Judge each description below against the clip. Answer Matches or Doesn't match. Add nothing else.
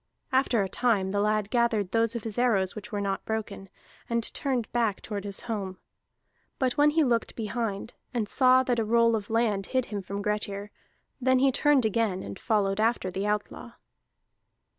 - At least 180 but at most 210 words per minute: Matches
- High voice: Matches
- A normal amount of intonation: Matches